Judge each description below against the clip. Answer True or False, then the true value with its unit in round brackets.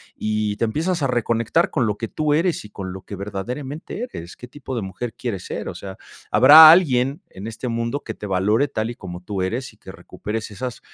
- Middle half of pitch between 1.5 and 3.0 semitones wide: False (5.0 semitones)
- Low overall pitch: True (115 Hz)